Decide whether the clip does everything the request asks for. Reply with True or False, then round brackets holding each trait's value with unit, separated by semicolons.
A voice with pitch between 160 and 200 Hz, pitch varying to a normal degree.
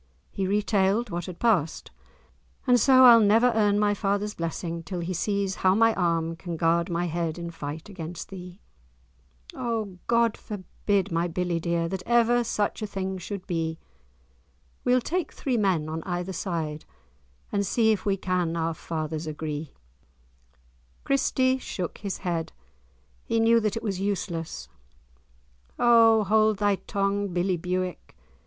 True (190 Hz; 4.1 semitones)